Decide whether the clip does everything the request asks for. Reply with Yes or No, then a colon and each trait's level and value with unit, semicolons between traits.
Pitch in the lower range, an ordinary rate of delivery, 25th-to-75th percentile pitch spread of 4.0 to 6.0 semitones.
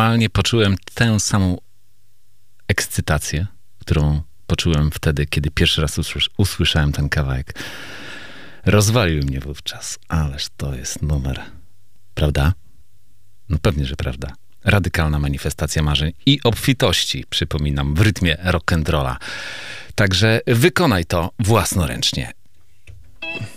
No: very low, 90 Hz; slow, 95 wpm; average, 5.3 semitones